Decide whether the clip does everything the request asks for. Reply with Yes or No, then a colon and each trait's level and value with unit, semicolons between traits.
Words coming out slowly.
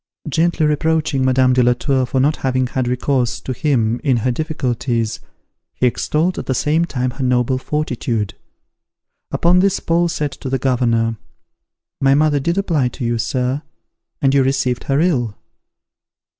No: average, 160 wpm